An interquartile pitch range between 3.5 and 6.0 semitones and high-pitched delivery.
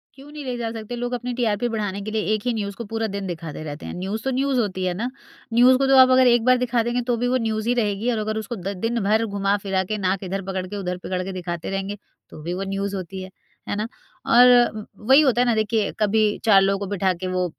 Yes: average, 3.8 semitones; high, 215 Hz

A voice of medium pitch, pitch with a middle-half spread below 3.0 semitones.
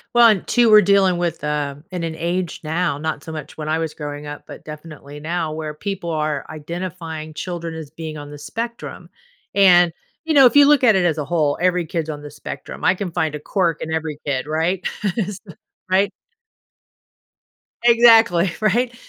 No: medium, 165 Hz; average, 3.9 semitones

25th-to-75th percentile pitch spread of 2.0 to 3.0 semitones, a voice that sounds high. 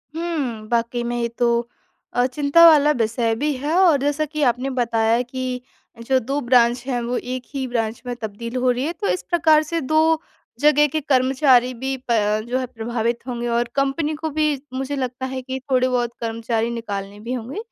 No: average, 3.4 semitones; very high, 255 Hz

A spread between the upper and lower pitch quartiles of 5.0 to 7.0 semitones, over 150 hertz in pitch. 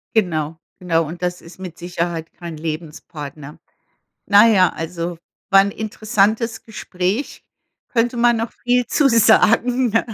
Yes: average, 5.3 semitones; medium, 185 Hz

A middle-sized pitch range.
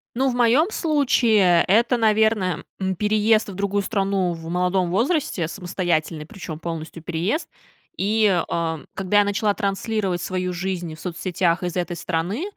Yes: average, 3.7 semitones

